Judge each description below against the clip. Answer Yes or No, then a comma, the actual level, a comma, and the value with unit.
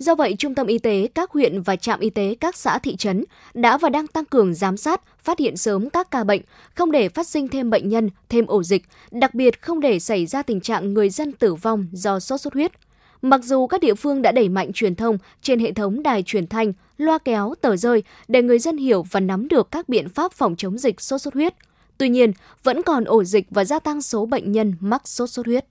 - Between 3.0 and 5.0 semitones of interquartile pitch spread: No, wide, 5.5 semitones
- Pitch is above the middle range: Yes, high, 235 Hz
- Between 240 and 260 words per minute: Yes, fast, 250 wpm